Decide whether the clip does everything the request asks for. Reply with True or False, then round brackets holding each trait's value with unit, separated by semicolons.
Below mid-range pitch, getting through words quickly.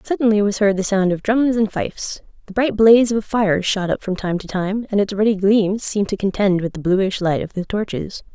False (205 Hz; 250 wpm)